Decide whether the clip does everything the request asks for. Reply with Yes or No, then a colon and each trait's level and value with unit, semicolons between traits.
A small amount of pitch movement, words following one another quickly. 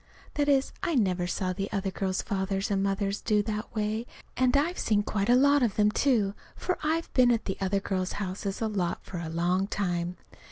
No: average, 3.9 semitones; fast, 210 wpm